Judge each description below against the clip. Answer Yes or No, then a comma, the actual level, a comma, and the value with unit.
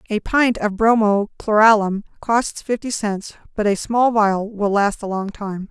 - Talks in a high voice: Yes, high, 210 Hz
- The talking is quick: No, average, 180 wpm